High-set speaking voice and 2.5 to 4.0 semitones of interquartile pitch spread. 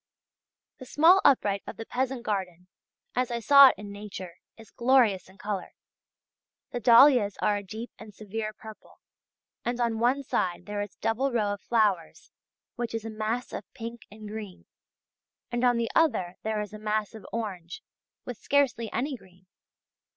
Yes: high, 220 Hz; average, 2.9 semitones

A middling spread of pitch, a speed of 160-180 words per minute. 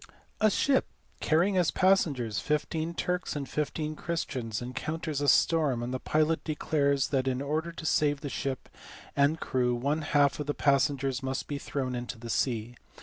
Yes: average, 3.5 semitones; average, 170 wpm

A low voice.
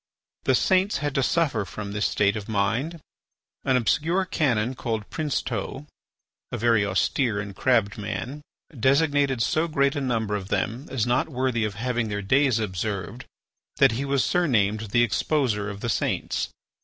Yes: low, 120 Hz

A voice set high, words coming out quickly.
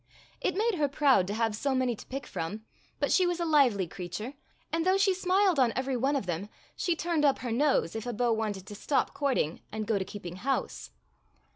Yes: very high, 255 Hz; fast, 230 wpm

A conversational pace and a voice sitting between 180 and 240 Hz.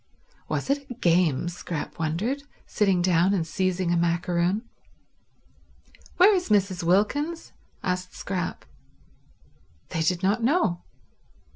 No: slow, 115 wpm; medium, 185 Hz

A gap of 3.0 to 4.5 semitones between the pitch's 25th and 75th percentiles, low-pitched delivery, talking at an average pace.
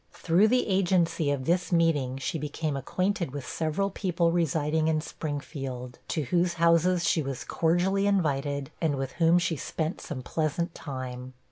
No: average, 3.6 semitones; medium, 160 Hz; average, 155 wpm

